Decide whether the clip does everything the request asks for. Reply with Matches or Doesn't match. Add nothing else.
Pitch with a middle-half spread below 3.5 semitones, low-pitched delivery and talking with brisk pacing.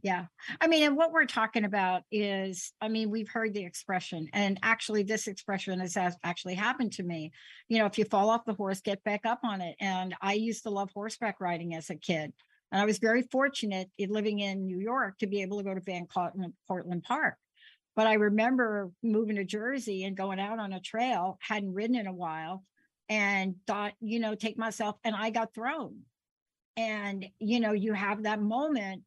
Doesn't match